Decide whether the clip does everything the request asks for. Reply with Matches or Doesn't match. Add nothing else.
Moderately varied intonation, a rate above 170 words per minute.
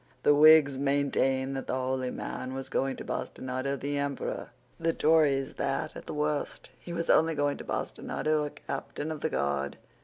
Doesn't match